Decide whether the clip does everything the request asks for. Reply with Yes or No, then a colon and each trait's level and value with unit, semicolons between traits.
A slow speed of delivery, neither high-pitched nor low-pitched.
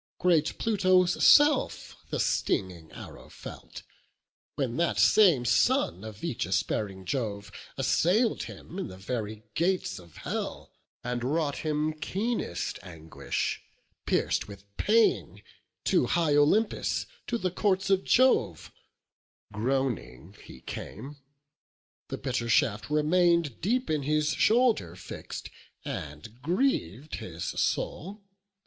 Yes: slow, 115 wpm; medium, 145 Hz